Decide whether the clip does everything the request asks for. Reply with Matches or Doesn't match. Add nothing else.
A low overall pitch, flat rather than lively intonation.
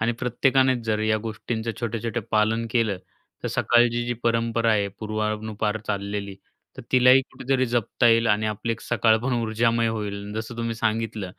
Matches